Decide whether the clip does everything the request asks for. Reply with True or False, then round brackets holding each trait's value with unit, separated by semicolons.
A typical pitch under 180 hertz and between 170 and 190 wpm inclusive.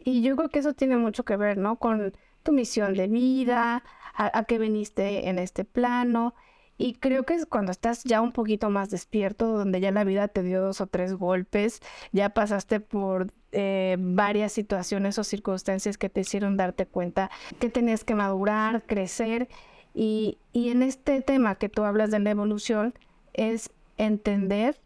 False (215 Hz; 180 wpm)